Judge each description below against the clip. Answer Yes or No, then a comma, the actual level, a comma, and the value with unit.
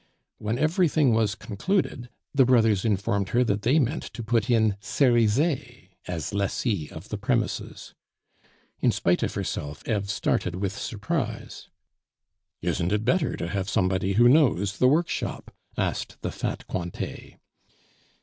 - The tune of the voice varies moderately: Yes, average, 4.5 semitones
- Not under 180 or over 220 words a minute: No, average, 140 wpm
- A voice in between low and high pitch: No, low, 110 Hz